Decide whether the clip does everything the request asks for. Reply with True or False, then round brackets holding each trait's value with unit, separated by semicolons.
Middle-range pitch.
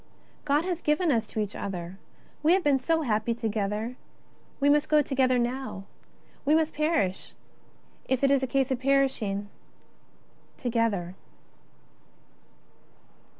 False (260 Hz)